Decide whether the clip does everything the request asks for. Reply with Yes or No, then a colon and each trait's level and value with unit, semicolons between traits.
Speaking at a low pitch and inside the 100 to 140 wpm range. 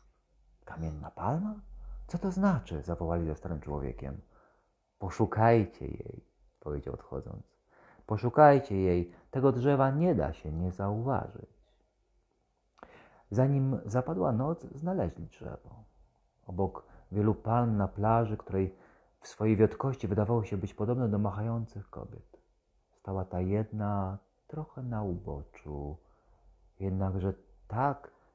Yes: low, 105 Hz; slow, 110 wpm